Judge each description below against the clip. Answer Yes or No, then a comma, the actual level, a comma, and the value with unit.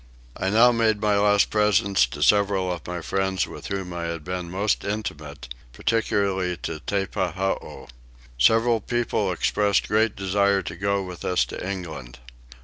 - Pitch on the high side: No, very low, 95 Hz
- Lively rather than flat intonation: No, narrow, 2.5 semitones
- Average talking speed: Yes, average, 150 wpm